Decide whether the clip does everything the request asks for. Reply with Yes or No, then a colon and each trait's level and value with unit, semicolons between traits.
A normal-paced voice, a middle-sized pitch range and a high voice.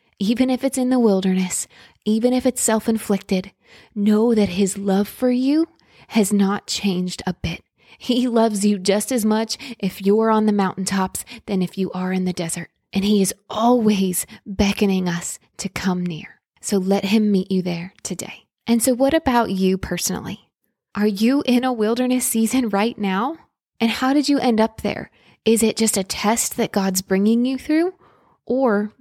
Yes: average, 180 wpm; average, 3.8 semitones; high, 210 Hz